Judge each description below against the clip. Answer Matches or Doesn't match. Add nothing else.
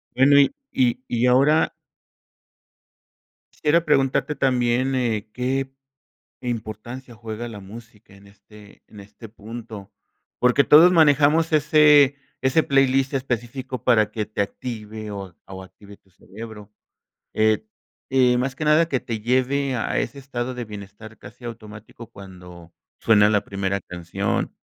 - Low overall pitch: Matches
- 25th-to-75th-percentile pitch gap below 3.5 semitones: Doesn't match